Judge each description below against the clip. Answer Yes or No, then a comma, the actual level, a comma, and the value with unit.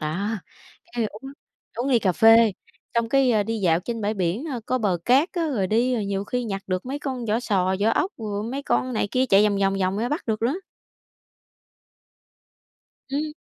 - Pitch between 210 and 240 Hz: Yes, high, 225 Hz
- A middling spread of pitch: Yes, average, 4.2 semitones